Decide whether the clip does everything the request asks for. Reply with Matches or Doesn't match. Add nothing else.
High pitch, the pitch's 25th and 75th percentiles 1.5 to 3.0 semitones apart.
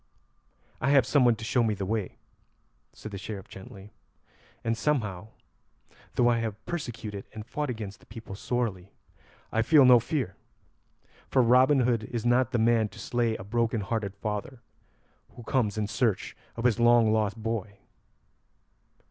Doesn't match